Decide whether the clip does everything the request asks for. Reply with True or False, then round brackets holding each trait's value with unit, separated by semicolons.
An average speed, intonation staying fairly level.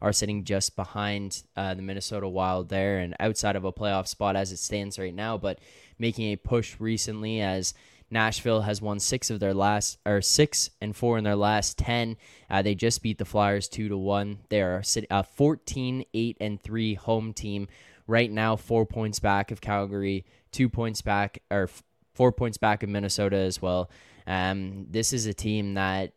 True (195 wpm; 2.3 semitones)